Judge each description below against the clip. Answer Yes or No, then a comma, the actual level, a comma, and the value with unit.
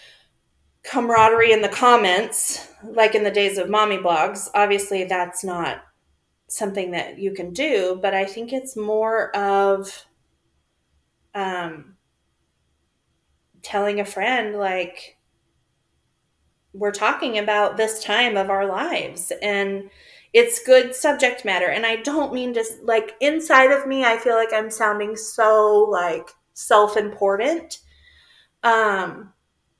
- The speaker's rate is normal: No, slow, 125 wpm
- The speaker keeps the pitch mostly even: No, average, 3.3 semitones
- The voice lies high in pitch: Yes, high, 205 Hz